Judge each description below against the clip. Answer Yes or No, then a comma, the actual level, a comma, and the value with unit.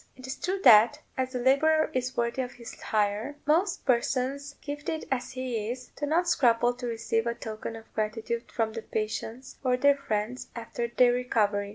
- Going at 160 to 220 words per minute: Yes, average, 185 wpm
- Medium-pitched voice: No, high, 245 Hz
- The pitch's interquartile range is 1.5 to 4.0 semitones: Yes, average, 3.3 semitones